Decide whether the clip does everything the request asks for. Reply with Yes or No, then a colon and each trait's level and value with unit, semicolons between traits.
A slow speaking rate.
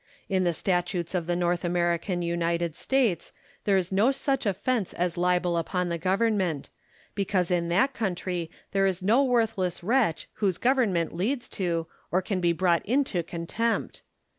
No: average, 160 wpm